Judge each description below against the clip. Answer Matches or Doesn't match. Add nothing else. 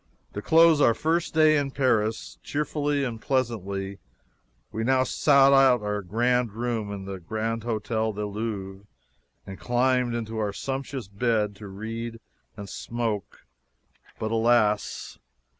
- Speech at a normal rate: Doesn't match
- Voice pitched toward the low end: Matches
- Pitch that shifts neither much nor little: Matches